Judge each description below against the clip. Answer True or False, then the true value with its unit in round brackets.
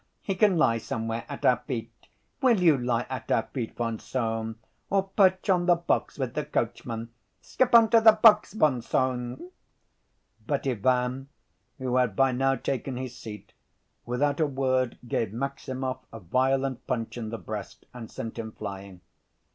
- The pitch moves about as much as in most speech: True (3.9 semitones)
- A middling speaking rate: True (165 wpm)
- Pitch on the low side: True (130 Hz)